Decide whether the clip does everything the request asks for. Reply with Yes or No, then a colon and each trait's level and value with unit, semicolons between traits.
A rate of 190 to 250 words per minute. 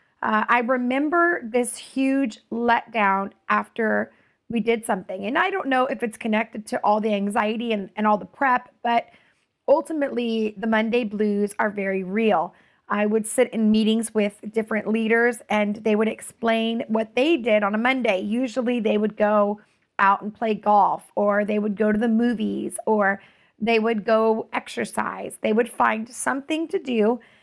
No: average, 170 wpm